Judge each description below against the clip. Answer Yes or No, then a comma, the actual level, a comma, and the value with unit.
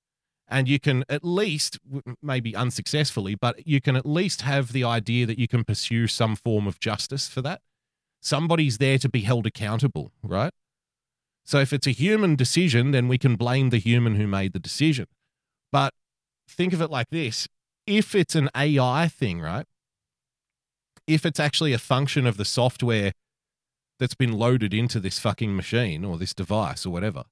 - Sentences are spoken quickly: No, average, 175 wpm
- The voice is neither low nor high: No, low, 130 Hz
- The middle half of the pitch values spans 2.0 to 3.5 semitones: No, average, 4.2 semitones